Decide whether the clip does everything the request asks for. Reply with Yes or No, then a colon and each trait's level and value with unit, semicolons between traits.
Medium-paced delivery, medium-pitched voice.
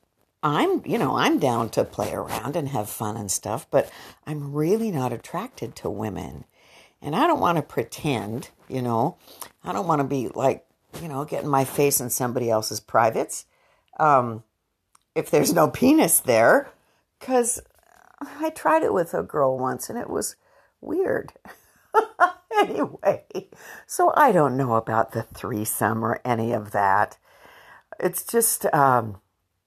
No: average, 155 wpm; low, 130 Hz